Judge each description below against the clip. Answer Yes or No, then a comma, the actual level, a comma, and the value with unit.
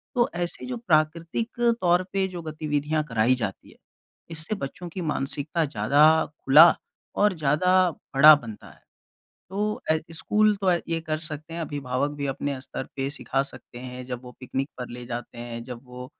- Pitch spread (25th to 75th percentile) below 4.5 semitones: No, average, 5.0 semitones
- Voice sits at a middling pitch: Yes, medium, 150 Hz